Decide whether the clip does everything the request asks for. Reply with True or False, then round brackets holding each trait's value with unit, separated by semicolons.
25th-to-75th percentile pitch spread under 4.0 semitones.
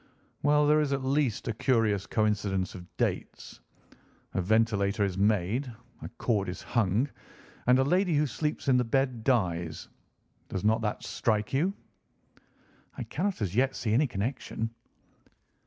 False (5.0 semitones)